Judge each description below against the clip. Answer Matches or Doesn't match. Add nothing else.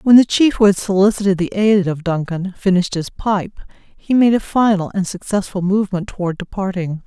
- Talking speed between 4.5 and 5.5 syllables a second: Matches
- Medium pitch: Doesn't match